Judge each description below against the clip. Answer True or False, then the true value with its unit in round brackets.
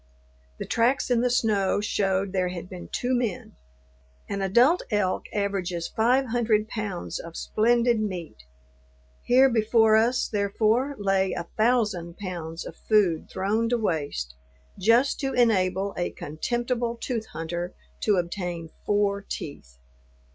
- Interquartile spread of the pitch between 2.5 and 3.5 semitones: False (4.3 semitones)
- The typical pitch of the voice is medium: False (205 Hz)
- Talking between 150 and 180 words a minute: False (135 wpm)